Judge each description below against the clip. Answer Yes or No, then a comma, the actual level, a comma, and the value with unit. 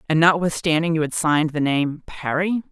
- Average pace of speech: Yes, average, 175 wpm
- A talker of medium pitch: Yes, medium, 160 Hz